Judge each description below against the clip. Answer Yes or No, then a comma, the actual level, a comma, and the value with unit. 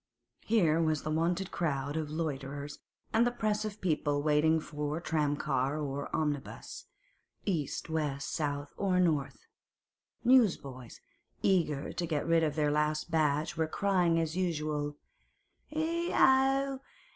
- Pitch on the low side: No, medium, 155 Hz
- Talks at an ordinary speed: No, slow, 125 wpm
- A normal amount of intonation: Yes, average, 3.8 semitones